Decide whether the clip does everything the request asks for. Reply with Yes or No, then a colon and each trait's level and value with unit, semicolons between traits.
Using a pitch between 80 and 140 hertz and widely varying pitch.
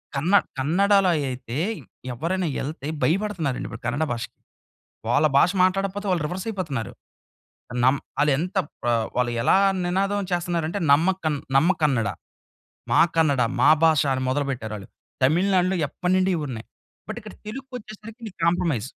No: medium, 165 Hz; wide, 5.8 semitones